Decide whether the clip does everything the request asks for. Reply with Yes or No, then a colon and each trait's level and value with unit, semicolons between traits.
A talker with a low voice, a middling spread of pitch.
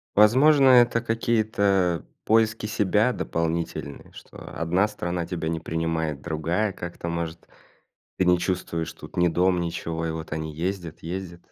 Yes: very low, 90 Hz; average, 4.2 semitones